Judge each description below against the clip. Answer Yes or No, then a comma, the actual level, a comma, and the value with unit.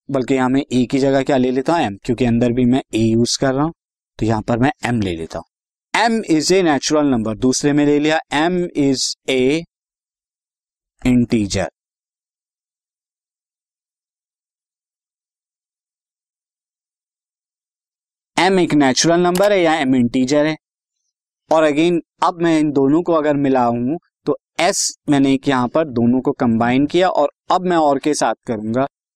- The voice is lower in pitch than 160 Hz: Yes, low, 135 Hz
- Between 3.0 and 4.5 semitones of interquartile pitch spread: Yes, average, 4.0 semitones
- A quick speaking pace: No, average, 160 wpm